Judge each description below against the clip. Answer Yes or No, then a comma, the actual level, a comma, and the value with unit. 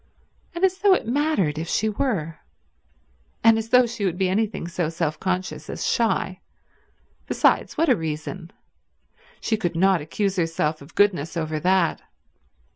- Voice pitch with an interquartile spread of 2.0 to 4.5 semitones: No, average, 5.3 semitones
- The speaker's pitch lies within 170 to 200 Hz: Yes, medium, 185 Hz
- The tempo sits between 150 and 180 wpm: Yes, average, 155 wpm